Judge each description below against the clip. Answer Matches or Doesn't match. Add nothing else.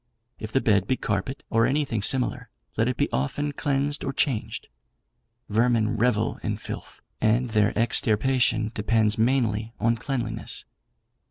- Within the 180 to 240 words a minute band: Doesn't match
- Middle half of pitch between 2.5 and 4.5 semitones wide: Matches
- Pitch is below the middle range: Matches